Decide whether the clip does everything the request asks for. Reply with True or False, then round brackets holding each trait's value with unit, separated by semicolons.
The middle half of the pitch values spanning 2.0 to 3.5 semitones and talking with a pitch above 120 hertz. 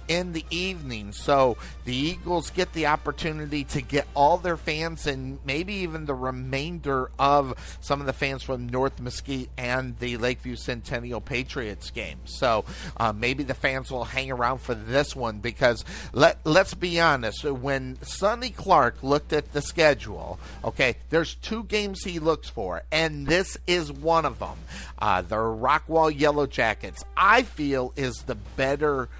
False (4.3 semitones; 140 Hz)